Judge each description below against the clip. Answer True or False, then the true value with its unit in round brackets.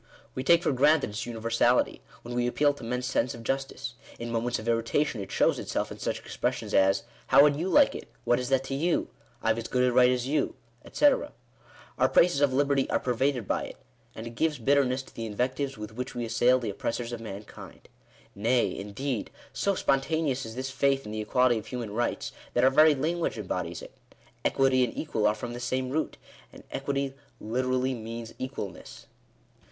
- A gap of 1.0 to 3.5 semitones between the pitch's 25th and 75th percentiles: True (3.0 semitones)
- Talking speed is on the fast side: True (210 wpm)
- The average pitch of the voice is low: True (125 Hz)